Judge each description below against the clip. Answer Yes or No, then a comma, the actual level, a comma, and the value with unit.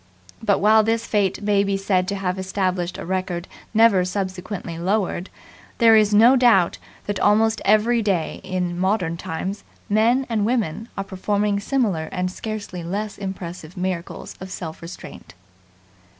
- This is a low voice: No, high, 195 Hz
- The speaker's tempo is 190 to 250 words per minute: No, average, 150 wpm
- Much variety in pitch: No, average, 2.9 semitones